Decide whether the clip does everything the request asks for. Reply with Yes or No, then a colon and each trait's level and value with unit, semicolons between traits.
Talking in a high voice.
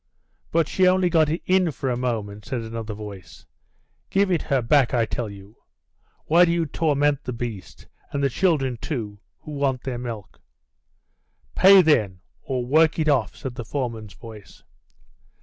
No: low, 130 Hz